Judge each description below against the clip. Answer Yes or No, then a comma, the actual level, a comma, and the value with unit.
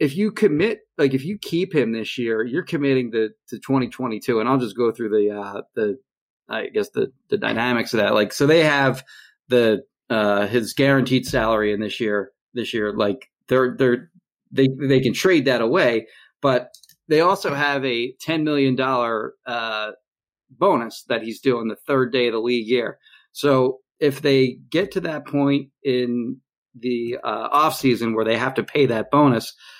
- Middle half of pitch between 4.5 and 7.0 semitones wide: No, average, 3.7 semitones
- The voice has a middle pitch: No, low, 130 Hz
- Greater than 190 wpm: No, average, 180 wpm